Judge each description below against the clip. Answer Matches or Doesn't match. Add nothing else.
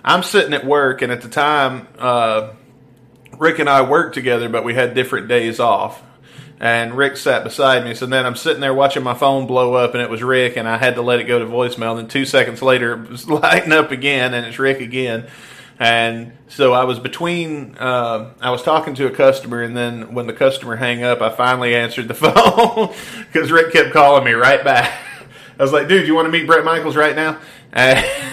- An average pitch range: Matches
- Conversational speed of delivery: Doesn't match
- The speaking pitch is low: Matches